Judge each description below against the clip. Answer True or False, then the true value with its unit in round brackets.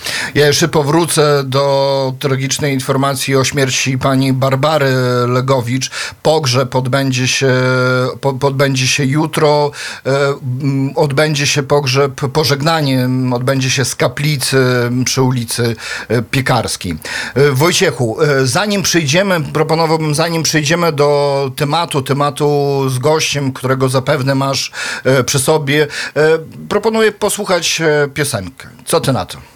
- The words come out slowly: True (105 wpm)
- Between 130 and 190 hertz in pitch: True (140 Hz)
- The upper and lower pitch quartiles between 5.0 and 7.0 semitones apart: False (2.5 semitones)